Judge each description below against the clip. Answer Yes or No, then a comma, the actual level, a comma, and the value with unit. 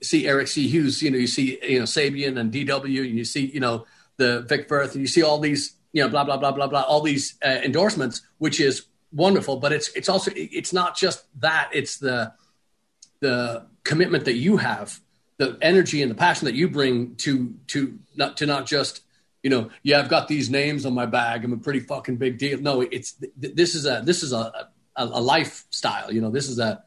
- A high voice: No, medium, 140 Hz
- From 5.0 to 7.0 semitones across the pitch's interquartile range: No, average, 2.7 semitones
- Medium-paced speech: No, fast, 230 wpm